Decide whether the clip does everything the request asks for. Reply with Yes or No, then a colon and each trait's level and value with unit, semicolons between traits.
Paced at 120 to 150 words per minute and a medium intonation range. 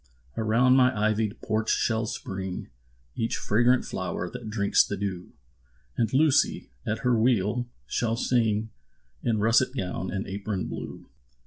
Yes: slow, 135 wpm; average, 3.0 semitones